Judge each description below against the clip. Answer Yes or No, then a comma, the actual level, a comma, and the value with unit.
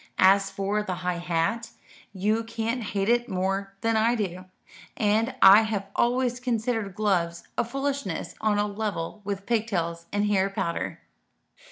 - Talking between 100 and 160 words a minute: Yes, average, 150 wpm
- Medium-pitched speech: No, high, 205 Hz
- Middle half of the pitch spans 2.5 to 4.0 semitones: Yes, average, 2.9 semitones